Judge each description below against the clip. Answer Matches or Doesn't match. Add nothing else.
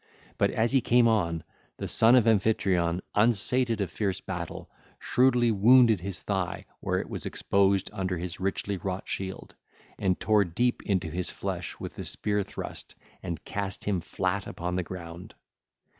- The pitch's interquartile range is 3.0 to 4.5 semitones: Matches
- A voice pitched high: Doesn't match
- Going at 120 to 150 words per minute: Doesn't match